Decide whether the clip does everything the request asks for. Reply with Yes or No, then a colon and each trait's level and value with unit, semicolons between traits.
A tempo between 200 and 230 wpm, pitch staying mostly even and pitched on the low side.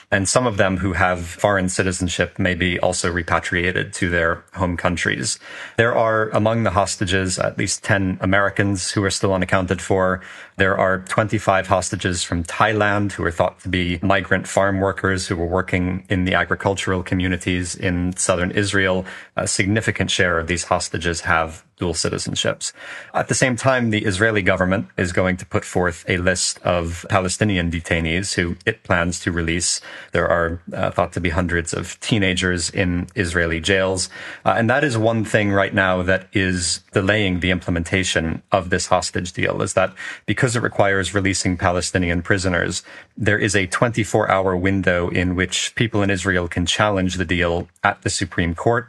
No: average, 175 wpm; narrow, 2.2 semitones; very low, 95 Hz